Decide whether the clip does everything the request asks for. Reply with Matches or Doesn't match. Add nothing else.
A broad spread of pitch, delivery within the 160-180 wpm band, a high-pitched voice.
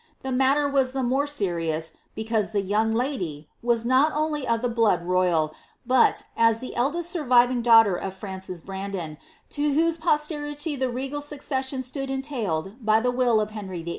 Matches